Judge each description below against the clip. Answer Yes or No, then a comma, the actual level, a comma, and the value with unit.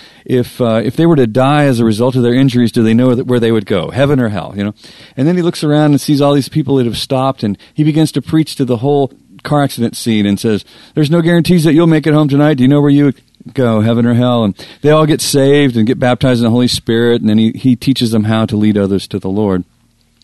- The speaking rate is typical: No, fast, 285 wpm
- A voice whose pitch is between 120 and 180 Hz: Yes, low, 125 Hz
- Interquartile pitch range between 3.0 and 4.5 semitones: Yes, average, 3.9 semitones